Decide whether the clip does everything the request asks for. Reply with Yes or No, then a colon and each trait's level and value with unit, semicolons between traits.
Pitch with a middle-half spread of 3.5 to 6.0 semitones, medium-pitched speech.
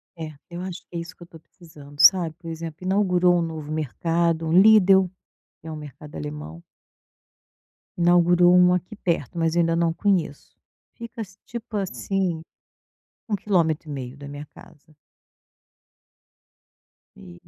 No: average, 2.8 semitones; medium, 170 Hz